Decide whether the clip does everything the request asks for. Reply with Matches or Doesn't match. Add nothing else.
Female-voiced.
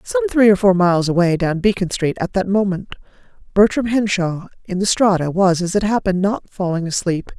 Matches